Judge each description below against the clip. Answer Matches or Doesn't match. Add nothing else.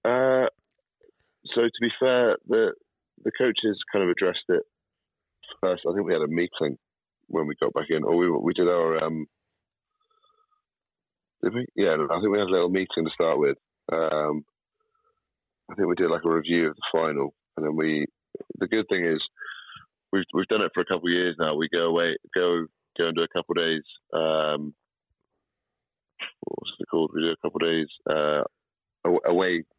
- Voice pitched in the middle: Doesn't match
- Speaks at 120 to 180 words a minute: Doesn't match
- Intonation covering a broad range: Matches